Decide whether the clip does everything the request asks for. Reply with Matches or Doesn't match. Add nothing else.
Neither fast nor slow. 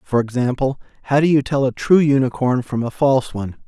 Doesn't match